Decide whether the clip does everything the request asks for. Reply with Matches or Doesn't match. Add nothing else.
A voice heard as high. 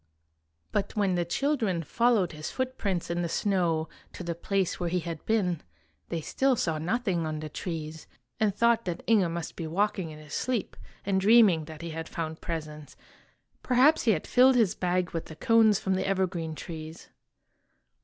Doesn't match